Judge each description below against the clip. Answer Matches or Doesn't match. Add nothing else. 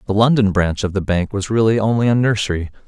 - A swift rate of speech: Matches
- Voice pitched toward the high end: Doesn't match